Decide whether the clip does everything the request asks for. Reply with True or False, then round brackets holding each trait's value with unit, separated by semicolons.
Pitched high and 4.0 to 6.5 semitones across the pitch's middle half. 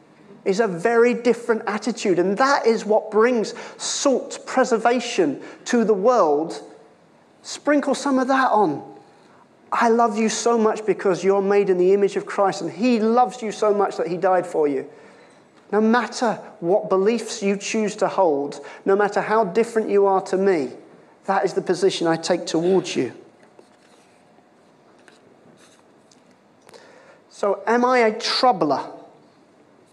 False (220 Hz; 3.4 semitones)